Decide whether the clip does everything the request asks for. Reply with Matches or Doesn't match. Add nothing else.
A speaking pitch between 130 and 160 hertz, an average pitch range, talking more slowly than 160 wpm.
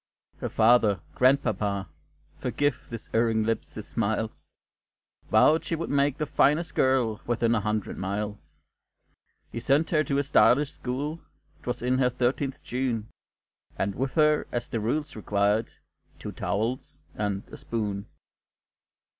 Doesn't match